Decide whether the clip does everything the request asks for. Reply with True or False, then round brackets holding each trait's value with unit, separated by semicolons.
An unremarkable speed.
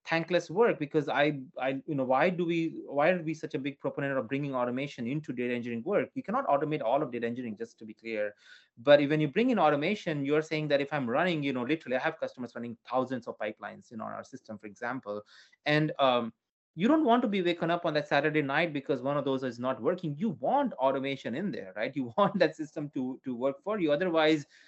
False (245 wpm)